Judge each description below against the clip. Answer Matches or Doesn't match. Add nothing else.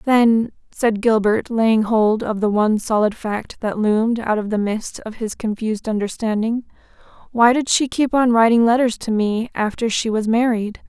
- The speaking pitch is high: Matches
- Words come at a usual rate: Matches